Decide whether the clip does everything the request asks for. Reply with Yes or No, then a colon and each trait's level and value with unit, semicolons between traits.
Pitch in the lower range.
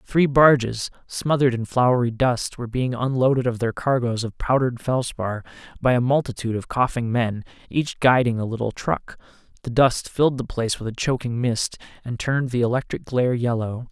Yes: low, 125 Hz